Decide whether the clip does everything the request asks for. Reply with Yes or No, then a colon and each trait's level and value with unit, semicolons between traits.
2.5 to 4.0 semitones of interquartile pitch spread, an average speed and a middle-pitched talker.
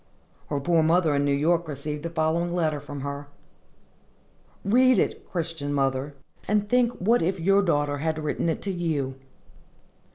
Yes: average, 3.6 semitones; average, 160 wpm; medium, 160 Hz